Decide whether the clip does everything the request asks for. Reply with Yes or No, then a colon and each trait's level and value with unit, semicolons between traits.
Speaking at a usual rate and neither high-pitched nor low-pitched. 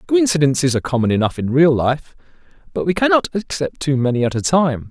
Yes: average, 195 wpm; medium, 150 Hz